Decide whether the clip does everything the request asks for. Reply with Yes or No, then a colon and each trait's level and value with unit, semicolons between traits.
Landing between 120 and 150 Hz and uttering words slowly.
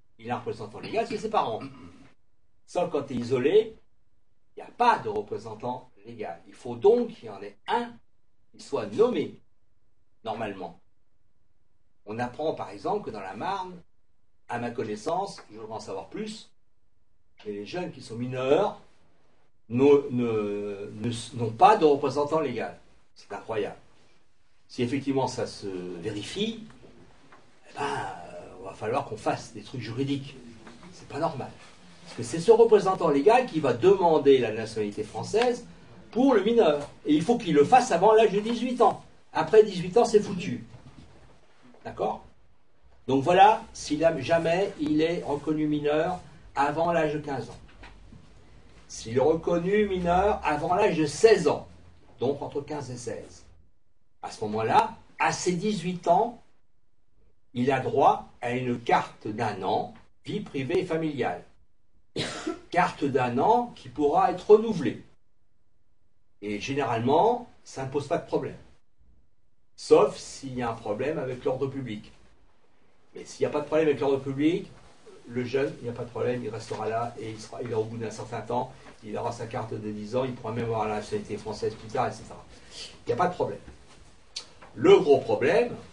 No: low, 135 Hz; average, 170 wpm